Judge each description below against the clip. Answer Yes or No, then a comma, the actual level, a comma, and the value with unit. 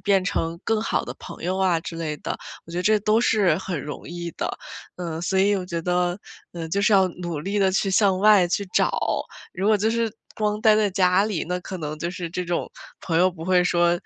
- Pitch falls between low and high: Yes, medium, 180 Hz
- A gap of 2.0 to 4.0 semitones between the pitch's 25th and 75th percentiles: Yes, average, 2.8 semitones